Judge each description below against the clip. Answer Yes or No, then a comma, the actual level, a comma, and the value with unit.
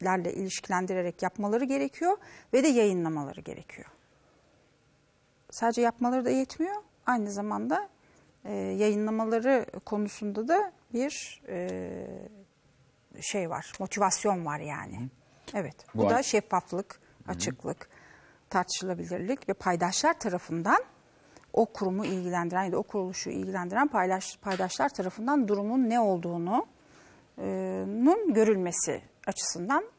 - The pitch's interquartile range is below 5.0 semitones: No, average, 5.3 semitones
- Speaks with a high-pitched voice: Yes, high, 200 Hz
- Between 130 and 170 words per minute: No, average, 100 wpm